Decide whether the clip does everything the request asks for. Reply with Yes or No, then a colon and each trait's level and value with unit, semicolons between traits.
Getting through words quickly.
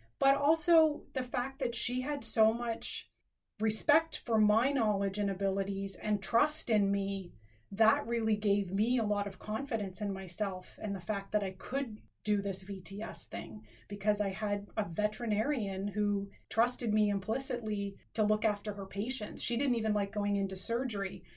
No: average, 170 wpm